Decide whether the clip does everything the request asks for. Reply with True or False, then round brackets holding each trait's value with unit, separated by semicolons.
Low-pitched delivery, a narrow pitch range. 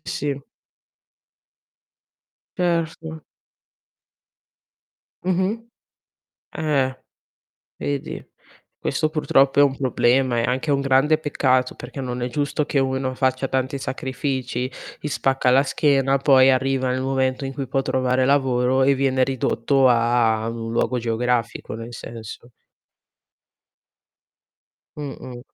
True (130 Hz; 1.8 semitones)